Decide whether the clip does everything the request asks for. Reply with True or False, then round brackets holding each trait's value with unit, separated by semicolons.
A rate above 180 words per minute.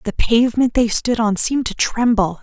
True (200 wpm)